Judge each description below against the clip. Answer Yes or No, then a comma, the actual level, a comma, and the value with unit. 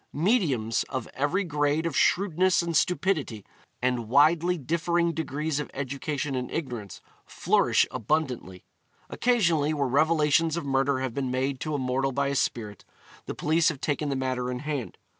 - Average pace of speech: Yes, average, 160 wpm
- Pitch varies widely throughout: No, average, 4.0 semitones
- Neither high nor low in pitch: Yes, medium, 145 Hz